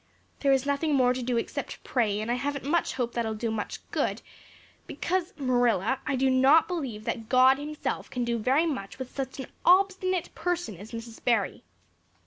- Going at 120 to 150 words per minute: No, average, 195 wpm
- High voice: Yes, very high, 260 Hz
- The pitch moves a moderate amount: Yes, average, 3.9 semitones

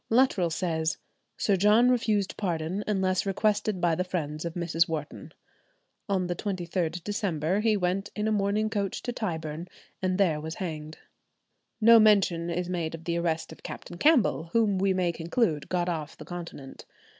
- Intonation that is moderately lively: Yes, average, 3.8 semitones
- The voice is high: No, medium, 180 Hz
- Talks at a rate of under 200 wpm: Yes, average, 170 wpm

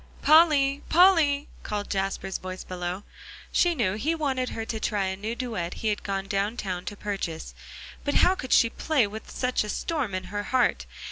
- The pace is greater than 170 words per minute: Yes, average, 190 wpm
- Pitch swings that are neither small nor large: No, wide, 6.2 semitones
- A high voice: Yes, high, 220 Hz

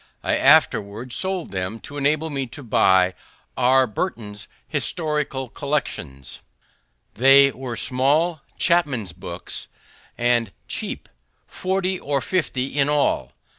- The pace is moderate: No, slow, 110 wpm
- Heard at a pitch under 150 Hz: Yes, low, 135 Hz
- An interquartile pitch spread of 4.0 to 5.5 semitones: Yes, average, 4.6 semitones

